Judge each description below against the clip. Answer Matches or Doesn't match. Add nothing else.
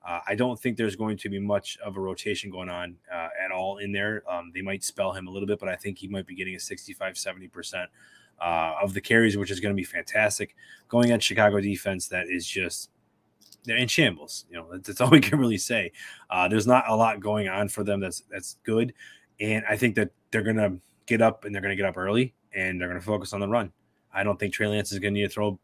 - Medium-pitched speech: Doesn't match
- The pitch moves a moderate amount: Doesn't match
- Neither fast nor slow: Doesn't match